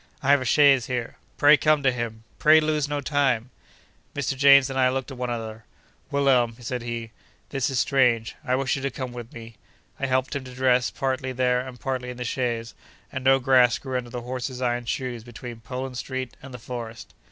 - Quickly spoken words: Yes, fast, 210 wpm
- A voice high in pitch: No, low, 130 Hz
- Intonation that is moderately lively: No, narrow, 1.8 semitones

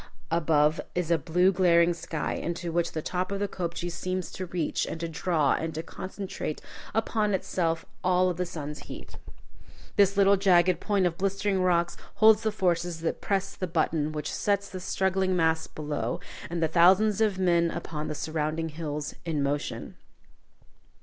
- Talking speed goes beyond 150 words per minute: Yes, average, 170 wpm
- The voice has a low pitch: No, medium, 175 Hz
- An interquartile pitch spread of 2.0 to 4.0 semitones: Yes, average, 2.8 semitones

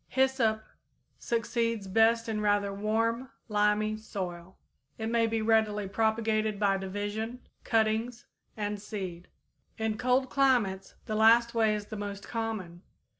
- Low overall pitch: No, high, 220 Hz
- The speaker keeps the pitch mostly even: Yes, narrow, 1.9 semitones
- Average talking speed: No, slow, 130 wpm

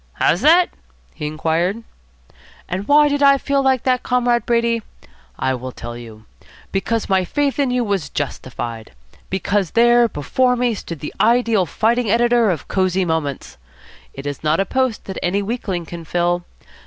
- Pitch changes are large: Yes, wide, 6.9 semitones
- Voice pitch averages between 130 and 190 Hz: No, high, 200 Hz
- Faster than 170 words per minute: No, average, 165 wpm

